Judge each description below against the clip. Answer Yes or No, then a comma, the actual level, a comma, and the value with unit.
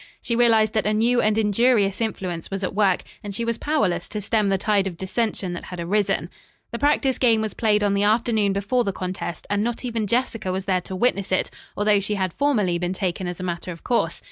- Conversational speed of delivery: No, fast, 230 wpm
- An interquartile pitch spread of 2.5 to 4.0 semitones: Yes, average, 3.4 semitones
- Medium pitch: No, high, 205 Hz